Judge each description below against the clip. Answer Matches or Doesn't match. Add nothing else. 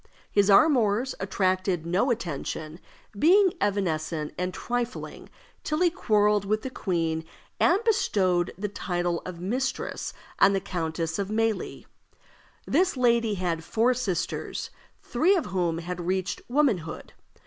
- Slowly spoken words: Matches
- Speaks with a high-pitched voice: Matches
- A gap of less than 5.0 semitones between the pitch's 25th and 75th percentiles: Doesn't match